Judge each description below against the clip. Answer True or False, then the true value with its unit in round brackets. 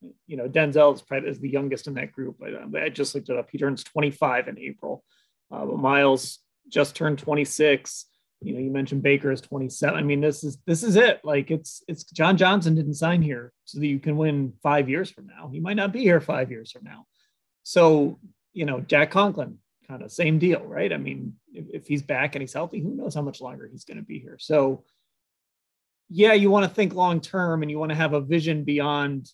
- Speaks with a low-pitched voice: False (150 Hz)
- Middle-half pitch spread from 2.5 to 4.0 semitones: True (2.9 semitones)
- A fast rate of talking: True (235 wpm)